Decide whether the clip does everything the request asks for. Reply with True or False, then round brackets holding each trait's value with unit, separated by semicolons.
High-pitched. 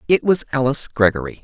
False (130 Hz)